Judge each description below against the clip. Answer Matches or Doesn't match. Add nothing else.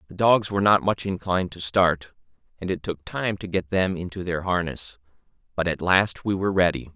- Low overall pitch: Matches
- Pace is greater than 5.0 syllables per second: Matches